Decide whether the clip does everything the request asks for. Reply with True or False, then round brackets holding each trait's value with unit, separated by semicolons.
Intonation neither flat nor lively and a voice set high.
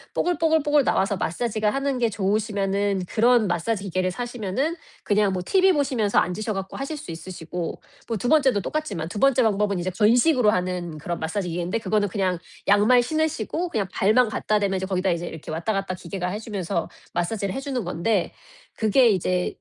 True (4.8 semitones; 205 Hz)